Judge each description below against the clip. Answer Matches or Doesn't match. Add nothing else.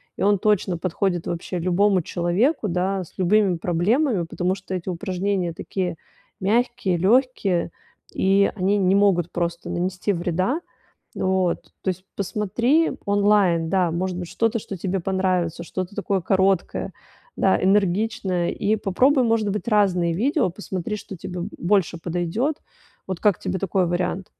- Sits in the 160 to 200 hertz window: Matches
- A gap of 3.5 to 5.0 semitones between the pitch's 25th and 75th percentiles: Doesn't match